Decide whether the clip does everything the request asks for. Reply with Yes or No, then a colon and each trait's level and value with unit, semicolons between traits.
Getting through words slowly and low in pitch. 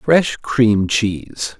Yes: slow, 115 wpm; low, 110 Hz